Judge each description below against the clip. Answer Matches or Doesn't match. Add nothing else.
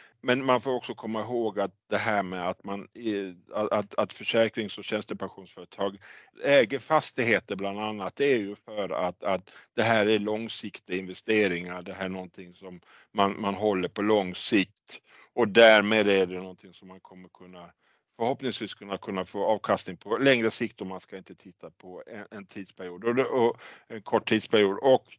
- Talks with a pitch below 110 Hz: Matches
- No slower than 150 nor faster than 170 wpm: Doesn't match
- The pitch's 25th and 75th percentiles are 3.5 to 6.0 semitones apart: Doesn't match